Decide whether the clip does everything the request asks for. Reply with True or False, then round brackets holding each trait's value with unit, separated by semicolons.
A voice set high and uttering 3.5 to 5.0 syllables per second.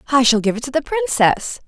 False (265 Hz; 5.9 syllables/s)